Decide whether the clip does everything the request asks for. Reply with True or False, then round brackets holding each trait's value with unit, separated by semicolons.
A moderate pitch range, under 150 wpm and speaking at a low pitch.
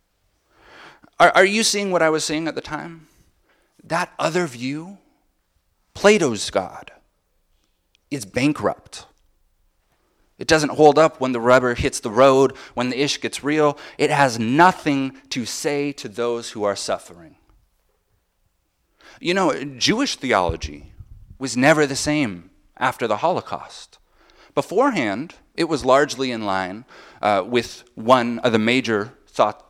False (6.7 semitones; 135 wpm; 130 Hz)